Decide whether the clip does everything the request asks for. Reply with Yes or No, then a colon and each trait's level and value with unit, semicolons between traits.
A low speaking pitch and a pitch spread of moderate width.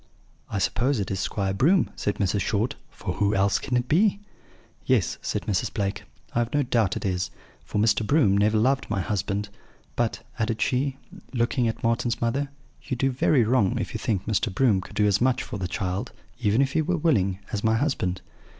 Yes: low, 110 Hz; average, 4.4 semitones